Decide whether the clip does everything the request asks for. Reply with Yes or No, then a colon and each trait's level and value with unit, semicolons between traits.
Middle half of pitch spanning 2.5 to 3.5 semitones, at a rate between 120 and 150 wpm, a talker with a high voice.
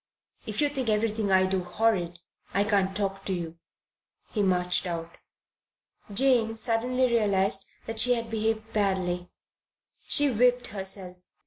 Yes: average, 3.2 semitones; slow, 135 wpm; high, 205 Hz